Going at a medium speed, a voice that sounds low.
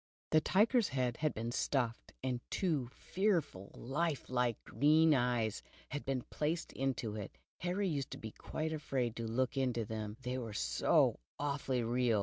Yes: average, 160 wpm; low, 130 Hz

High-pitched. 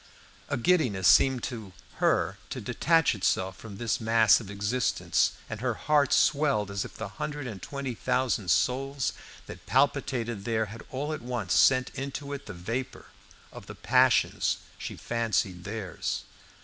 No: low, 120 Hz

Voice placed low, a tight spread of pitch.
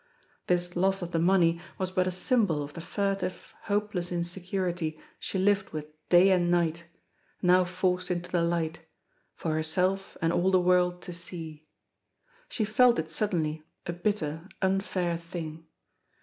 No: medium, 180 Hz; narrow, 2.2 semitones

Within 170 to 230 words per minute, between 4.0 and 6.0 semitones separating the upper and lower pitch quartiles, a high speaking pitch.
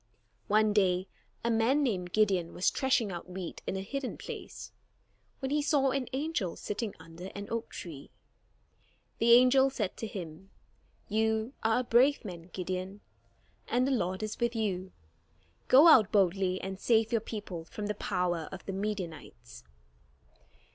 No: average, 155 wpm; average, 4.4 semitones; high, 210 Hz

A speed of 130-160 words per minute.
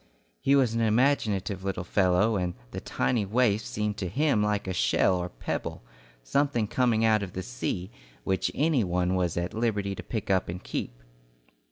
No: average, 185 wpm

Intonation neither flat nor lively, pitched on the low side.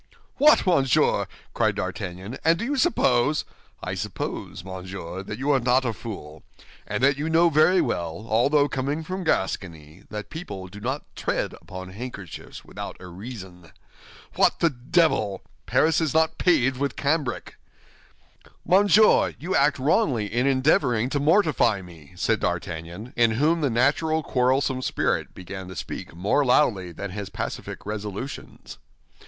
No: wide, 7.8 semitones; low, 125 Hz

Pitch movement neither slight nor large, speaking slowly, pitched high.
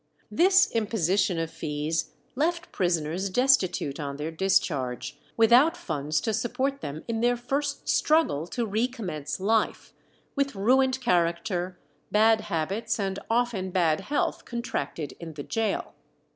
No: wide, 6.9 semitones; slow, 130 wpm; high, 200 Hz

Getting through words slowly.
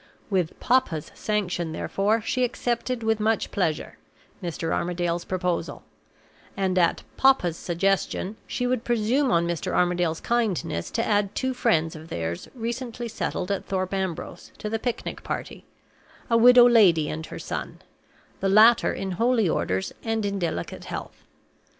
No: average, 145 wpm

